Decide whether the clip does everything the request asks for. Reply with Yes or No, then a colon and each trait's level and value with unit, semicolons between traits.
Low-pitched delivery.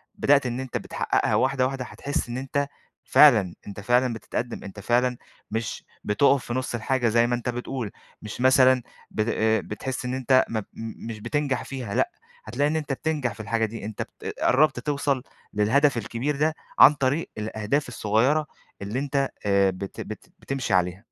Yes: low, 125 Hz